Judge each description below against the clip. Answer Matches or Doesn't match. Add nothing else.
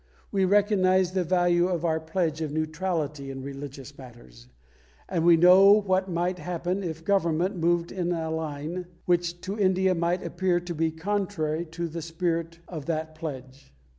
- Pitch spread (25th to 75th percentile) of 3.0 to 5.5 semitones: Doesn't match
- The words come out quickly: Doesn't match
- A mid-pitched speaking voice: Matches